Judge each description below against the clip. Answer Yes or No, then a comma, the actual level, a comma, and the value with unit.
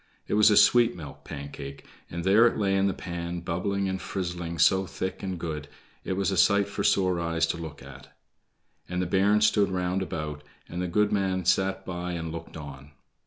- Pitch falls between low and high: No, very low, 90 Hz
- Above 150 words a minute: Yes, average, 200 wpm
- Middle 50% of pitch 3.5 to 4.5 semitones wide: No, average, 2.8 semitones